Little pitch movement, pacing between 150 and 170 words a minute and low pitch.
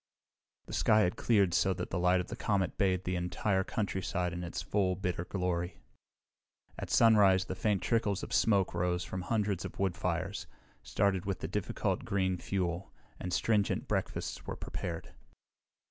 Yes: narrow, 2.1 semitones; average, 165 wpm; very low, 95 Hz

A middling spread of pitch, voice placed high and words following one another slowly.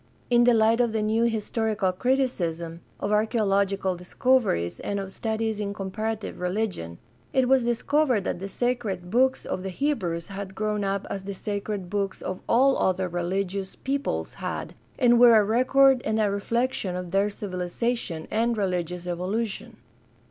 No: average, 3.9 semitones; high, 205 Hz; average, 165 wpm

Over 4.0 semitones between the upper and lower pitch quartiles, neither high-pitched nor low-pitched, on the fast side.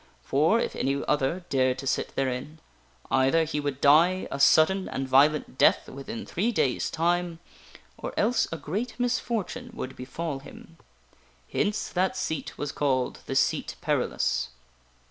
No: wide, 5.5 semitones; medium, 150 Hz; average, 150 wpm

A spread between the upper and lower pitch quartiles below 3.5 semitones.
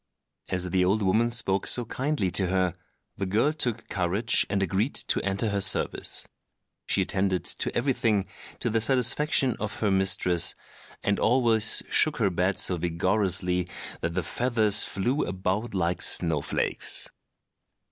No: average, 3.9 semitones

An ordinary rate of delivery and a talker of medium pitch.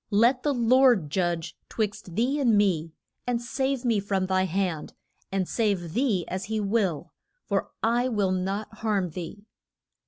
No: average, 155 wpm; high, 205 Hz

